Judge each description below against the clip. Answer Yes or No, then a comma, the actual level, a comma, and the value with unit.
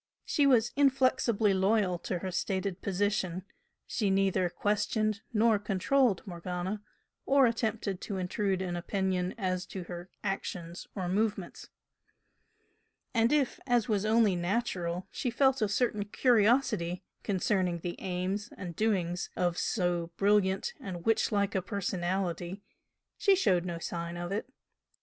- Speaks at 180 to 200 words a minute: No, slow, 135 wpm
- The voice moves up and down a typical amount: Yes, average, 3.5 semitones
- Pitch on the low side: No, high, 195 Hz